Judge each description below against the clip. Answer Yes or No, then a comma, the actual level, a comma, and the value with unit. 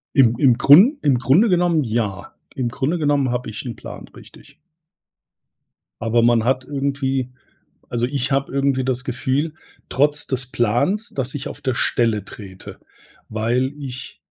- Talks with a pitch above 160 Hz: No, low, 130 Hz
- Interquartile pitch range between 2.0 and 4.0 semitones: Yes, average, 2.9 semitones